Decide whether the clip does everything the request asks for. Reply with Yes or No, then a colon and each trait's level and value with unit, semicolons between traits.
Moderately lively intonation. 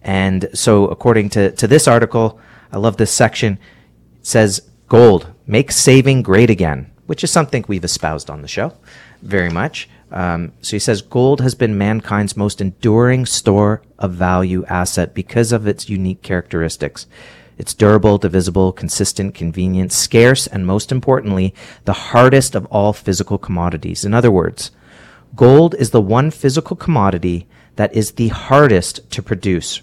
Yes: average, 4.1 semitones